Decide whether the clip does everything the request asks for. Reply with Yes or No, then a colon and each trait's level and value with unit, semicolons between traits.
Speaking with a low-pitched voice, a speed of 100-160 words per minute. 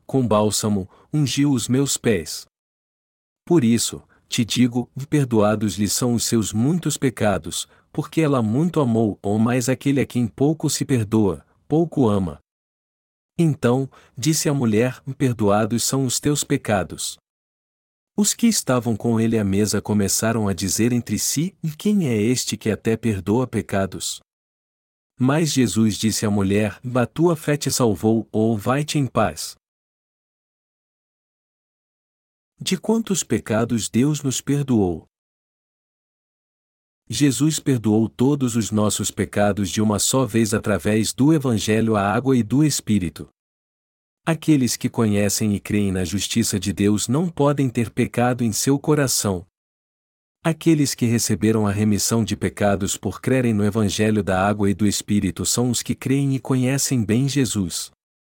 Yes: low, 115 Hz; average, 140 wpm